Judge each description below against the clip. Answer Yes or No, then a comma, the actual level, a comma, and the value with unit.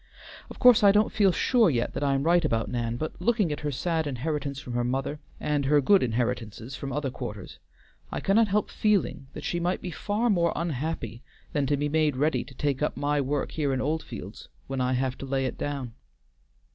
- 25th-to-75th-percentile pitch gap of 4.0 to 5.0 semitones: Yes, average, 4.6 semitones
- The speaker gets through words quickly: Yes, fast, 215 wpm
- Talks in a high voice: No, medium, 145 Hz